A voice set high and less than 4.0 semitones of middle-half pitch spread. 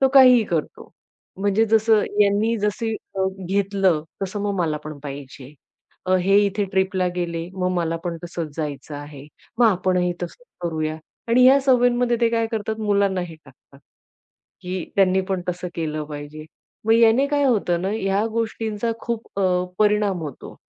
No: high, 195 Hz; average, 4.9 semitones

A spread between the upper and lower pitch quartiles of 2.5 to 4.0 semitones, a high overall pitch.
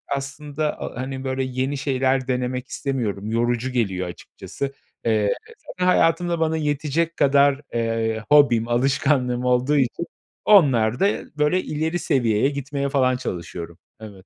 No: average, 3.6 semitones; low, 130 Hz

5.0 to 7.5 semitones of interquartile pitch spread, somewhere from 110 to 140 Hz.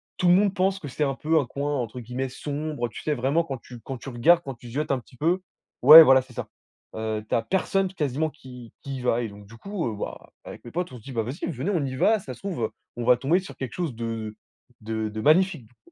Yes: wide, 5.4 semitones; low, 135 Hz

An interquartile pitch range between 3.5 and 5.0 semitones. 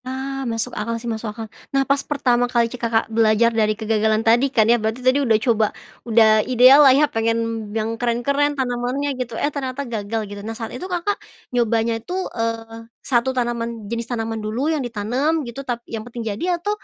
No: average, 2.8 semitones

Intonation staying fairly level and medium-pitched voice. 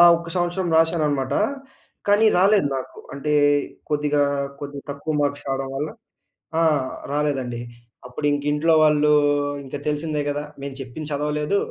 Yes: narrow, 2.0 semitones; medium, 150 Hz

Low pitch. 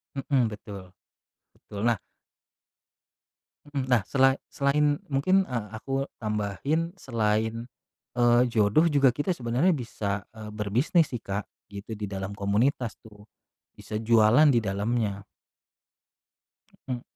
Yes: low, 115 Hz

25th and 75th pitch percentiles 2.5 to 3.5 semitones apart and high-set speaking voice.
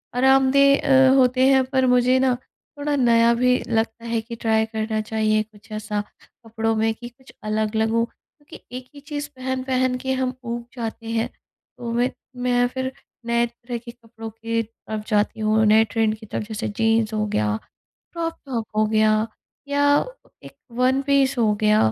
Yes: average, 2.8 semitones; high, 235 Hz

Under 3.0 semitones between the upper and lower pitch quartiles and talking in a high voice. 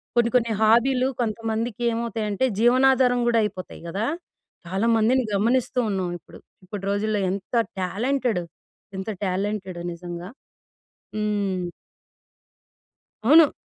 No: average, 3.7 semitones; high, 220 Hz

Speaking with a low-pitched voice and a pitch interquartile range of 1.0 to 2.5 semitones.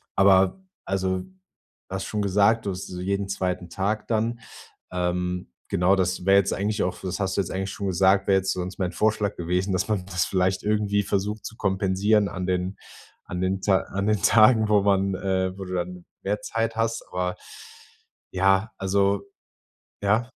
Yes: very low, 95 Hz; narrow, 1.8 semitones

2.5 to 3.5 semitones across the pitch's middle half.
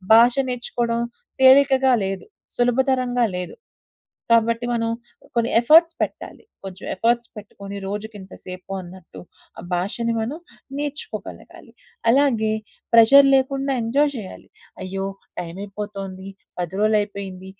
No: average, 4.7 semitones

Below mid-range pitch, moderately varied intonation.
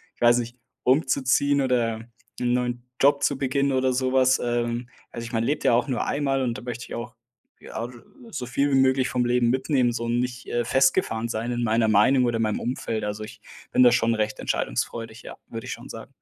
No: low, 120 Hz; narrow, 1.9 semitones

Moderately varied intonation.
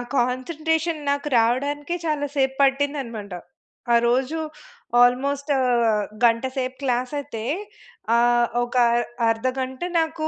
Yes: average, 3.2 semitones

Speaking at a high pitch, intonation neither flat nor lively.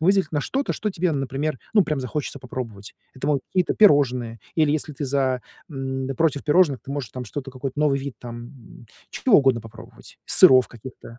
No: low, 135 Hz; average, 3.1 semitones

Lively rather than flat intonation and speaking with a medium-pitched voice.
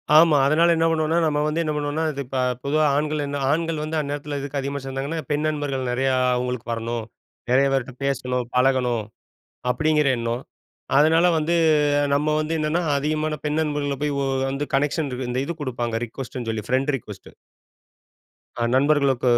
No: average, 2.9 semitones; medium, 145 Hz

